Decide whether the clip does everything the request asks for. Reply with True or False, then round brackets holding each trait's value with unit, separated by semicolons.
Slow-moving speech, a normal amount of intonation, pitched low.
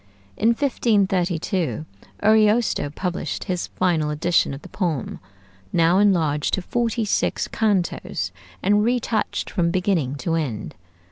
False (120 wpm; 4.5 semitones; 180 Hz)